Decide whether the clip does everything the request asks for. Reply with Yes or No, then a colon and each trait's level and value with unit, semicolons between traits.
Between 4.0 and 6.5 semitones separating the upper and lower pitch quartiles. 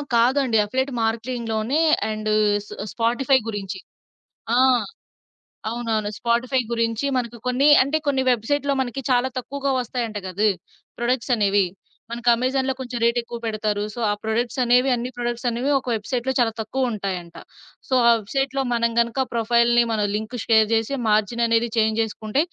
No: narrow, 2.5 semitones